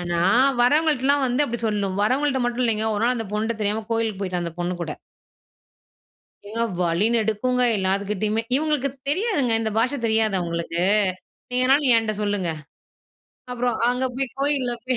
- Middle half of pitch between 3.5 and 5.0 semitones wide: Yes, average, 3.9 semitones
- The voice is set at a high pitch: Yes, high, 225 Hz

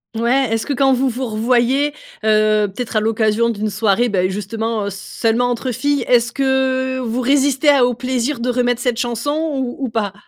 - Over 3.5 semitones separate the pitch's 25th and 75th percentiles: No, average, 2.9 semitones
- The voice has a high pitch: Yes, high, 240 Hz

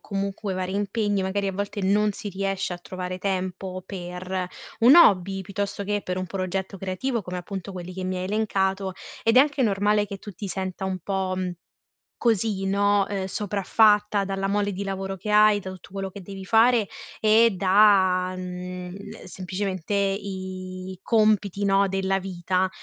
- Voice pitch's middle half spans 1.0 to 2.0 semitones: Yes, narrow, 1.7 semitones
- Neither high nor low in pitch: No, high, 195 Hz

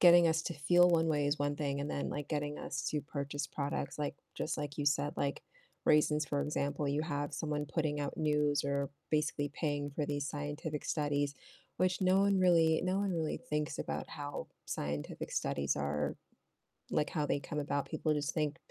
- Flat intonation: Yes, narrow, 1.6 semitones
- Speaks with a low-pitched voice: No, medium, 150 Hz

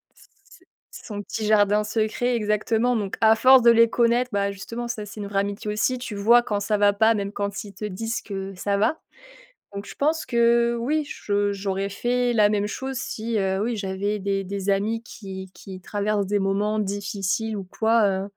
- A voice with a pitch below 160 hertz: No, high, 210 Hz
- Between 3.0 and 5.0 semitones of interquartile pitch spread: No, narrow, 2.5 semitones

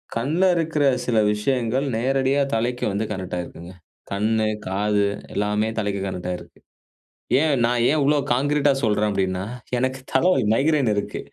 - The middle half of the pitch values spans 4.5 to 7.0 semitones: Yes, average, 5.1 semitones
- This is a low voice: Yes, low, 115 Hz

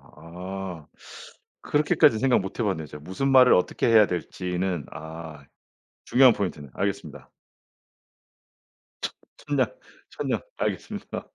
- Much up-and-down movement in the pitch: Yes, wide, 6.0 semitones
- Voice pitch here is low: Yes, very low, 95 Hz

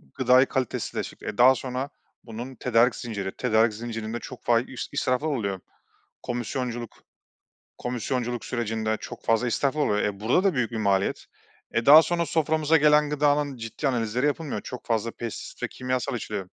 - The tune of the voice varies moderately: Yes, average, 3.3 semitones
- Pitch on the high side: No, low, 120 Hz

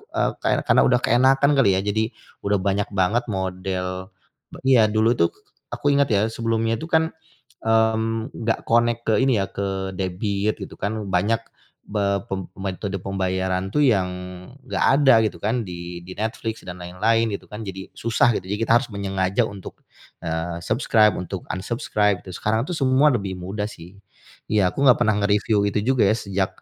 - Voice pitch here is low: Yes, low, 105 Hz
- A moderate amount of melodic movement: Yes, average, 3.2 semitones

